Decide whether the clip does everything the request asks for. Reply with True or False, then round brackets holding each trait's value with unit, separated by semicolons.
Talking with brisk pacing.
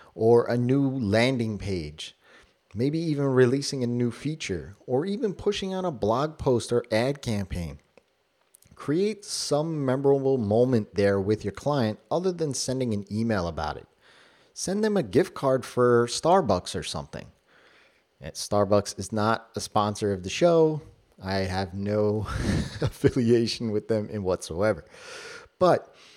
False (140 wpm)